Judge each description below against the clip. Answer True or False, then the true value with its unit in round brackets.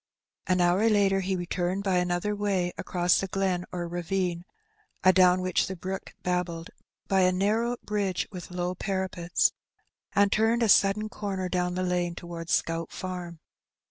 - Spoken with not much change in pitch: True (1.7 semitones)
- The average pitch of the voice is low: False (185 Hz)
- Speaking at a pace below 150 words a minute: False (155 wpm)